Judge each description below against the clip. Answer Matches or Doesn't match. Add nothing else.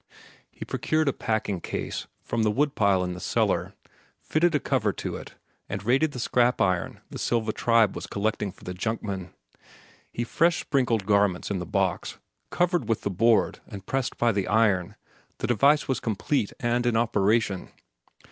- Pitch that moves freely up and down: Doesn't match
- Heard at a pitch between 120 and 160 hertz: Doesn't match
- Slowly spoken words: Doesn't match